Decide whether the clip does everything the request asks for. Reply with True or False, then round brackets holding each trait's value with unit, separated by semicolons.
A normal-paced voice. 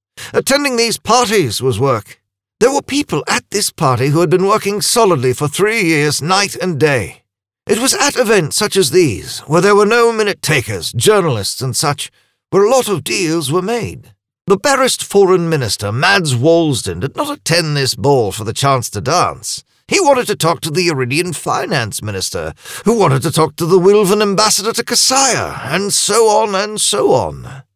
True (185 wpm)